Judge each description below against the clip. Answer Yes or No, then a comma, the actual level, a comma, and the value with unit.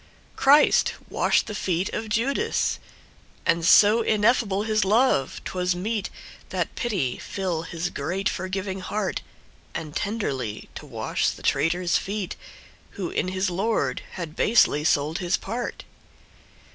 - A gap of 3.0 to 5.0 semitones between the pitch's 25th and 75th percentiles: Yes, average, 4.0 semitones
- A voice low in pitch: No, high, 190 Hz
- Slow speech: Yes, slow, 115 wpm